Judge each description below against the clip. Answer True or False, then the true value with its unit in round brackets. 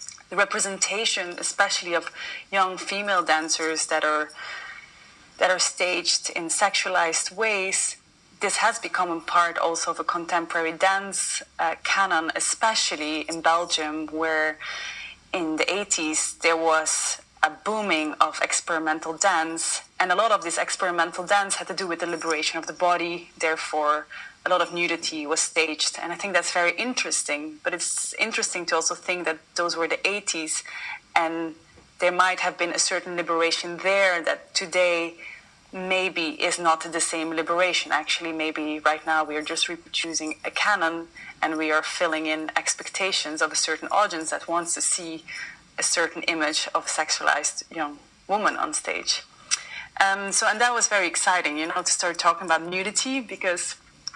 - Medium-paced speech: True (165 wpm)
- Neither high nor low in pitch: True (175 Hz)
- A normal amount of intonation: True (3.0 semitones)